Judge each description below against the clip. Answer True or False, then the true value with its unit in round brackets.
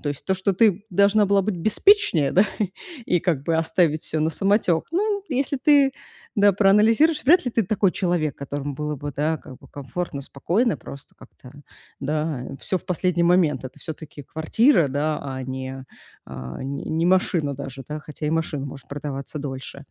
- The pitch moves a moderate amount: False (5.8 semitones)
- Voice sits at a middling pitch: True (160 Hz)